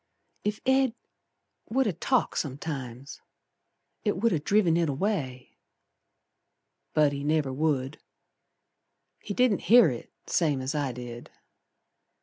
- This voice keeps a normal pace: No, slow, 120 wpm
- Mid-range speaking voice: Yes, medium, 155 Hz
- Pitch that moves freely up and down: Yes, wide, 7.6 semitones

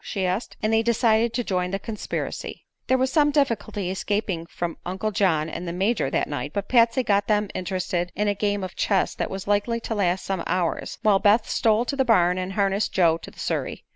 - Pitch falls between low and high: No, high, 200 Hz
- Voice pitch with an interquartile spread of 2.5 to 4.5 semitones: Yes, average, 3.4 semitones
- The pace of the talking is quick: Yes, fast, 220 wpm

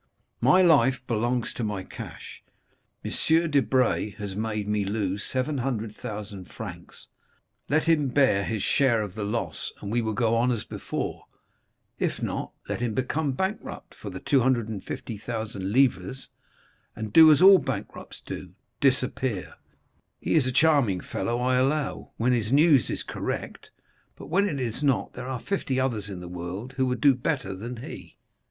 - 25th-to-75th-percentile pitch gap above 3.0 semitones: Yes, average, 4.3 semitones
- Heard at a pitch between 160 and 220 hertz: No, low, 120 Hz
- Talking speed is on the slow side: No, average, 160 wpm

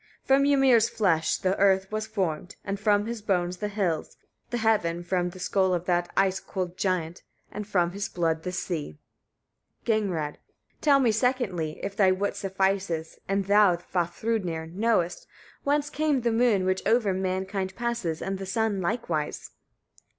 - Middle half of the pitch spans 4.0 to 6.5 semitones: No, average, 3.6 semitones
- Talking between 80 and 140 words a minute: No, average, 165 wpm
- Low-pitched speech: No, high, 195 Hz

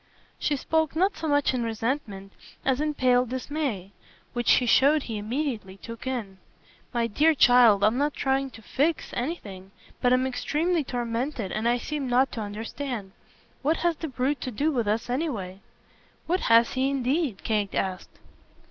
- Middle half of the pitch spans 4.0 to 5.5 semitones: Yes, average, 4.6 semitones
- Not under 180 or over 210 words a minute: No, average, 165 wpm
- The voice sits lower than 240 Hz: No, very high, 250 Hz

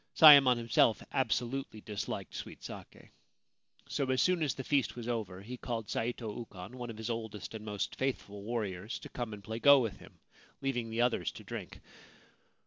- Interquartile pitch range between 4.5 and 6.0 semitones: No, average, 3.0 semitones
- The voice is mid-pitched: No, low, 115 Hz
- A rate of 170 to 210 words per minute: Yes, average, 180 wpm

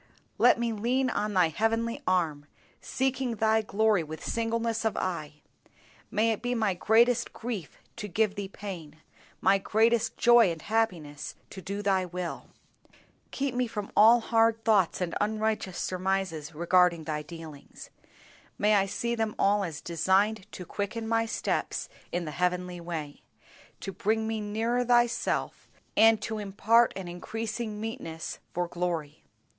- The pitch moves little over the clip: No, average, 4.1 semitones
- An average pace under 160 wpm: Yes, average, 150 wpm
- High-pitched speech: Yes, high, 205 Hz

